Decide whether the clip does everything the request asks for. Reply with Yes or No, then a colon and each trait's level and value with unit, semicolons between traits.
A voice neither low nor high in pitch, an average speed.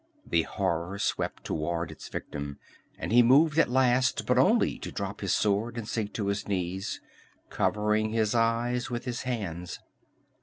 No: low, 110 Hz; average, 160 wpm